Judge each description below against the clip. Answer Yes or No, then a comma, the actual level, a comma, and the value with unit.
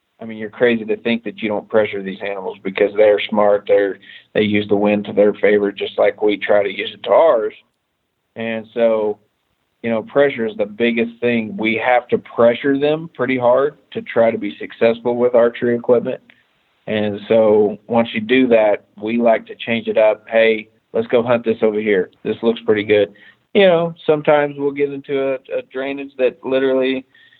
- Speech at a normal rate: Yes, average, 195 wpm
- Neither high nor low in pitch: No, low, 115 Hz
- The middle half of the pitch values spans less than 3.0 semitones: No, average, 3.7 semitones